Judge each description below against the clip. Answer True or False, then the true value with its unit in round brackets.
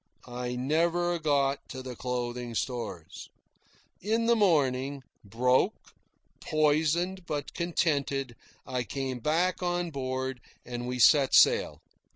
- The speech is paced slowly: True (115 wpm)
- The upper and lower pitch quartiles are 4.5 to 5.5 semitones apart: True (4.9 semitones)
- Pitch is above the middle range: False (135 Hz)